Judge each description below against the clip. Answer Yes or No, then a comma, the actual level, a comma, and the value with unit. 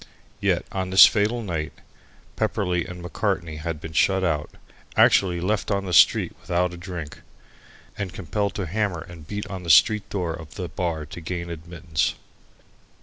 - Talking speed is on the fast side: No, average, 165 wpm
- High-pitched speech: No, very low, 90 Hz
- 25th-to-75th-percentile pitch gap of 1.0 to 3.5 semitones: Yes, average, 2.8 semitones